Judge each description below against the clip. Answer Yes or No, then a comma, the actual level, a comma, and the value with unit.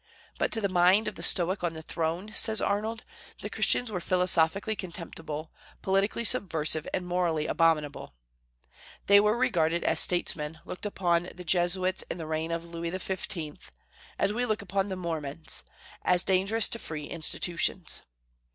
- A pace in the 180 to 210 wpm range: No, average, 155 wpm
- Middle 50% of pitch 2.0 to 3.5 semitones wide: Yes, average, 3.2 semitones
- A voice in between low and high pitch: Yes, medium, 180 Hz